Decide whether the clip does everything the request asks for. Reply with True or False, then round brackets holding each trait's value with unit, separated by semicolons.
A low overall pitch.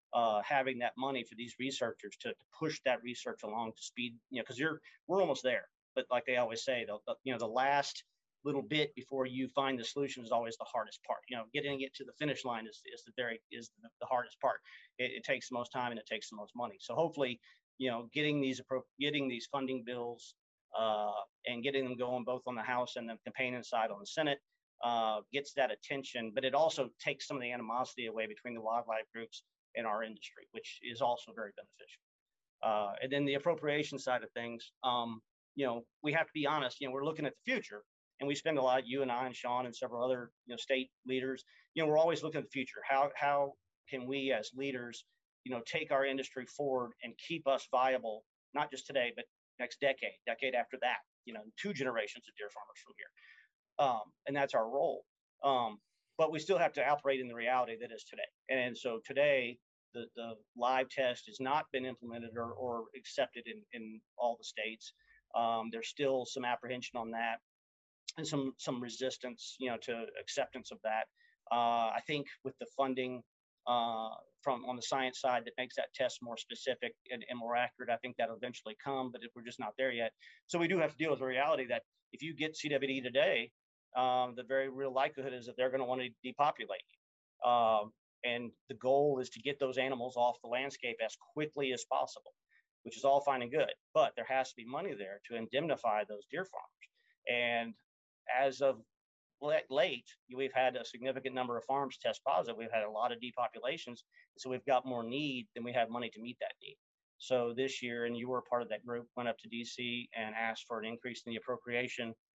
True (125 Hz)